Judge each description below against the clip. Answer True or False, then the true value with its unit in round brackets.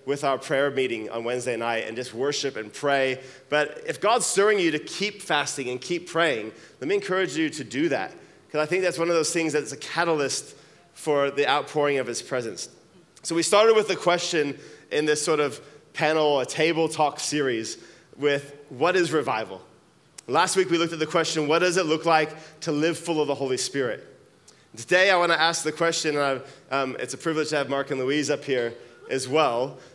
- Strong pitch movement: False (3.3 semitones)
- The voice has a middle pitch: True (150 Hz)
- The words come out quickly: True (210 wpm)